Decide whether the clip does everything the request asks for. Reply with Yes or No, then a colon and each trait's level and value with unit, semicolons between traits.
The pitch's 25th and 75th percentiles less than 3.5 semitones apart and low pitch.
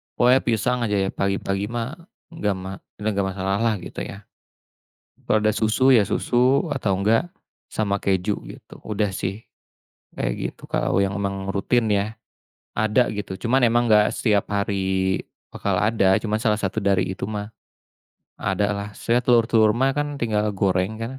Yes: average, 2.7 semitones; low, 105 Hz